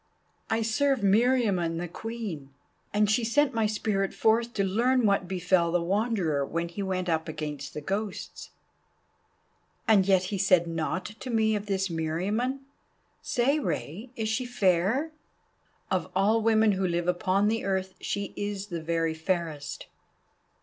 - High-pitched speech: Yes, high, 195 Hz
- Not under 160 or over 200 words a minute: No, average, 150 wpm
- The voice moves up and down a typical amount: Yes, average, 4.5 semitones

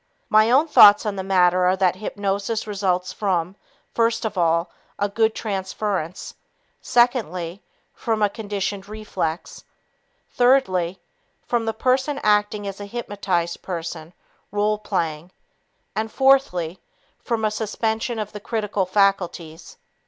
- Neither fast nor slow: No, slow, 125 wpm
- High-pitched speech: Yes, high, 205 Hz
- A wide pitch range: No, average, 3.2 semitones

